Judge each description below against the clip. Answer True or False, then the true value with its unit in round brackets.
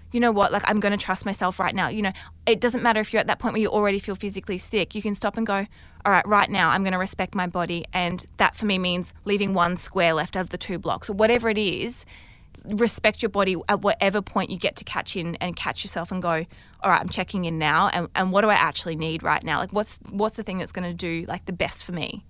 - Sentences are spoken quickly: True (285 wpm)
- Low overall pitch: False (195 Hz)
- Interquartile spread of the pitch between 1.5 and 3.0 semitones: True (2.7 semitones)